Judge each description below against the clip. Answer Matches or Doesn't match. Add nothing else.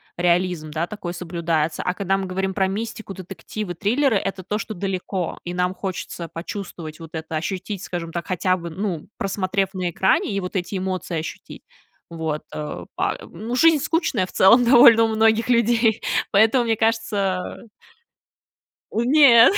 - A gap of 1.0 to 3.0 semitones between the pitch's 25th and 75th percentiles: Doesn't match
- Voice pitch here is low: Doesn't match